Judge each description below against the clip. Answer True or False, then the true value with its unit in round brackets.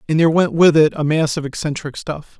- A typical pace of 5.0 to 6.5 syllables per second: True (6.0 syllables/s)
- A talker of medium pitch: True (155 Hz)